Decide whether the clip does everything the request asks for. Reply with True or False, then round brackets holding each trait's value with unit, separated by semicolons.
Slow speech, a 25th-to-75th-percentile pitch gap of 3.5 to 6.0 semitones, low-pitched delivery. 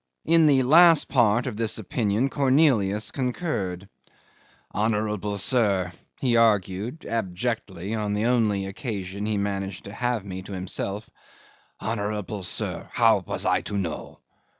True (130 wpm; 3.8 semitones; 105 Hz)